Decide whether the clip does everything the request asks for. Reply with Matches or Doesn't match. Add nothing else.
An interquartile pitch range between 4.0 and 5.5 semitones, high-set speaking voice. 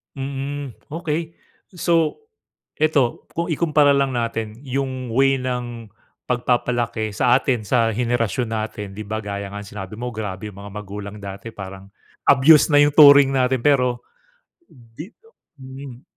Doesn't match